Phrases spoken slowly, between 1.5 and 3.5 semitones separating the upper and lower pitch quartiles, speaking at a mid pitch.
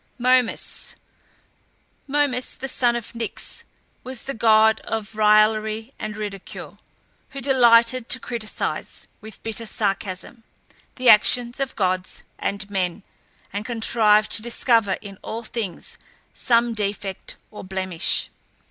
No: slow, 120 wpm; narrow, 2.5 semitones; high, 220 Hz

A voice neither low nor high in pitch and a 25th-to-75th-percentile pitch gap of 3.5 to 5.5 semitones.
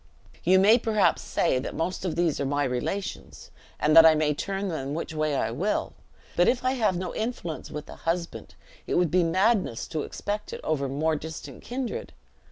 Yes: medium, 170 Hz; average, 4.4 semitones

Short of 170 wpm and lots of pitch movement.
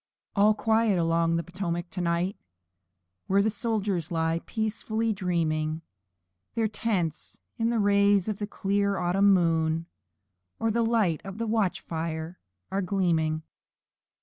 No: slow, 135 wpm; average, 4.2 semitones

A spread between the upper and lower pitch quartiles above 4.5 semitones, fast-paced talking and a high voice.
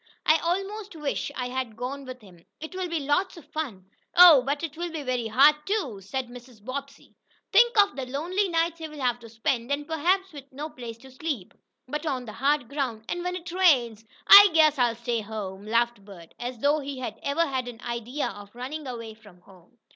Yes: average, 5.1 semitones; fast, 215 wpm; very high, 270 Hz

